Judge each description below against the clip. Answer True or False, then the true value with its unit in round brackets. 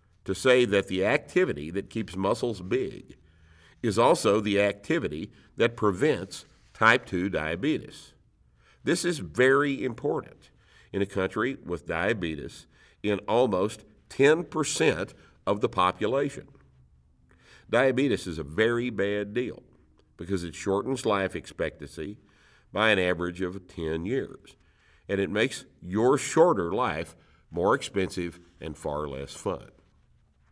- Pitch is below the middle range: True (95 Hz)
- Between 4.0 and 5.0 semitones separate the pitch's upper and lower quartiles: True (4.6 semitones)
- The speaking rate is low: True (120 wpm)